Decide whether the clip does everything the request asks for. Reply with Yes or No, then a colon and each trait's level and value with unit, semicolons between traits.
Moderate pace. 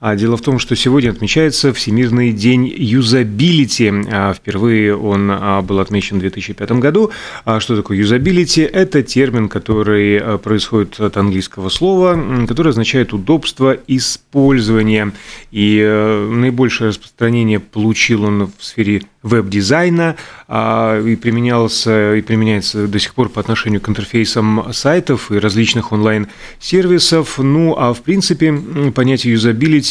Yes: average, 120 wpm